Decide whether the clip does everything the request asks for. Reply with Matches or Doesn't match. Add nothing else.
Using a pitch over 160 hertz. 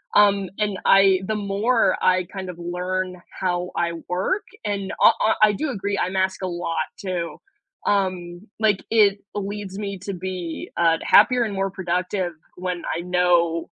Matches